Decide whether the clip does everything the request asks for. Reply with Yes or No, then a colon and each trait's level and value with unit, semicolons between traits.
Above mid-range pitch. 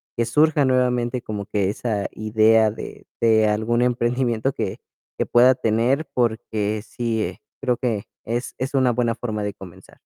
No: low, 115 Hz